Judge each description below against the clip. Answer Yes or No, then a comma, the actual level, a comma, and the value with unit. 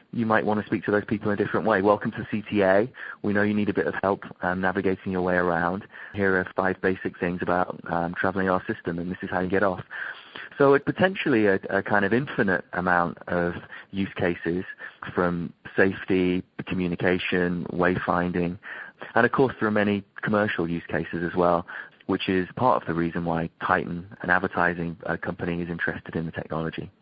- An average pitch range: Yes, average, 3.0 semitones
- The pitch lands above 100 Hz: No, very low, 95 Hz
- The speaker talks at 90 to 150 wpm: No, average, 195 wpm